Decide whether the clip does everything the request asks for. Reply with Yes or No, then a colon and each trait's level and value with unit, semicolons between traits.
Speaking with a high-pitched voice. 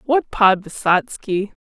Yes: high, 210 Hz